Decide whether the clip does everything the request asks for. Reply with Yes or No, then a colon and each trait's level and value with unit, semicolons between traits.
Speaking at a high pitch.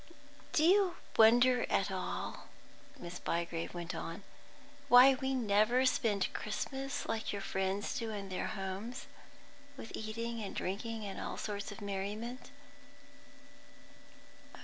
Yes: high, 215 Hz